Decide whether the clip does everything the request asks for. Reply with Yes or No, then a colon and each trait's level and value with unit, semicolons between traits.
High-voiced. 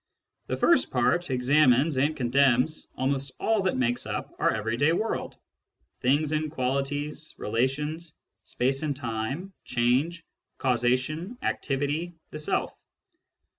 No: medium, 140 Hz